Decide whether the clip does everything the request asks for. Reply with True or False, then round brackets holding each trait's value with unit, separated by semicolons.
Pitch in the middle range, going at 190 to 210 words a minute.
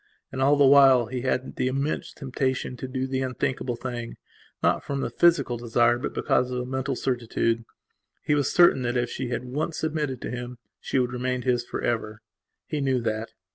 False (130 Hz; 200 wpm)